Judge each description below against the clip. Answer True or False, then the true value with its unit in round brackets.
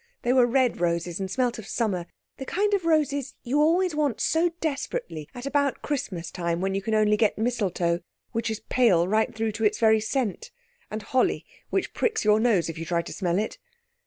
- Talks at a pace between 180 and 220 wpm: True (200 wpm)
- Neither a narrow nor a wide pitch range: False (6.1 semitones)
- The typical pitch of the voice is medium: False (220 Hz)